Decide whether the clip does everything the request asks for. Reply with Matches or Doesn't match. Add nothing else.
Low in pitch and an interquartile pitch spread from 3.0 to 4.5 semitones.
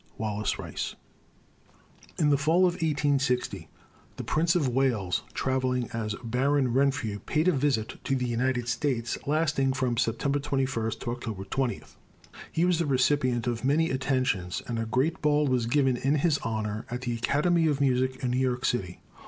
Matches